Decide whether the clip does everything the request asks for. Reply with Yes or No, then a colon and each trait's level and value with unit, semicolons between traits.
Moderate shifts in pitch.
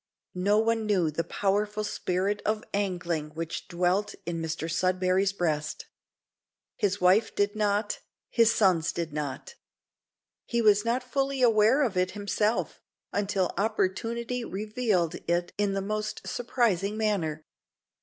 Yes: average, 3.3 semitones